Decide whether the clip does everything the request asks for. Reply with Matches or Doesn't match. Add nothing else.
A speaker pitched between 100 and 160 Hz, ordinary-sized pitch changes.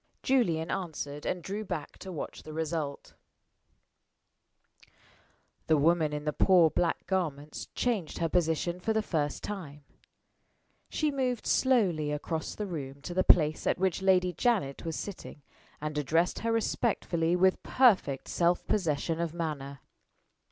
Doesn't match